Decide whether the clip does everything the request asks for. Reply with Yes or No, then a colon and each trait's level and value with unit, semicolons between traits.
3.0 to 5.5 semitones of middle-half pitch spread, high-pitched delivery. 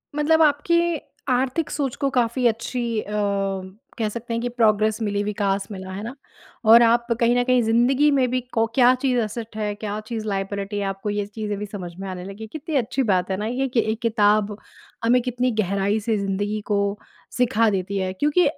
Yes: average, 3.4 semitones; high, 225 Hz